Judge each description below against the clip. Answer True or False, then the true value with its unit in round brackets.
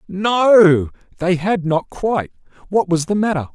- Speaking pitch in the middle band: True (180 Hz)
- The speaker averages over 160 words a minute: False (150 wpm)